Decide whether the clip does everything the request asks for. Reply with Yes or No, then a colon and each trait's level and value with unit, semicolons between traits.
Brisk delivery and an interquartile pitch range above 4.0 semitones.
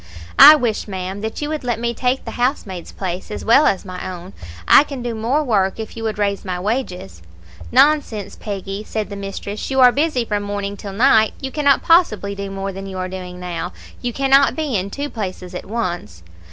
Yes: fast, 210 wpm; average, 4.7 semitones